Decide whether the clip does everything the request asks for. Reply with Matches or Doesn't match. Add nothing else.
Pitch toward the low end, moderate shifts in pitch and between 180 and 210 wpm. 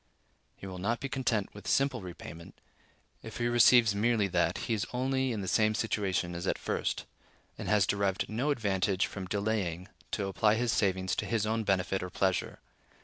Matches